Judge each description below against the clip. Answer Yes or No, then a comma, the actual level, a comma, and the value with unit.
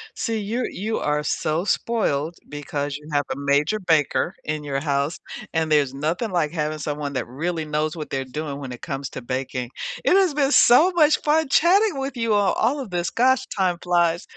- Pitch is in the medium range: Yes, medium, 160 Hz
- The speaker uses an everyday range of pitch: No, wide, 7.7 semitones